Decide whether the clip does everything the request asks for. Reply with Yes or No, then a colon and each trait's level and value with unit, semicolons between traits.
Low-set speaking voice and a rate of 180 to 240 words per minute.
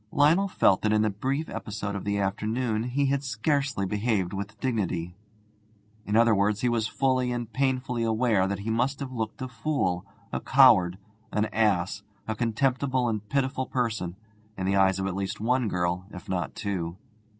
Yes: low, 110 Hz; average, 185 wpm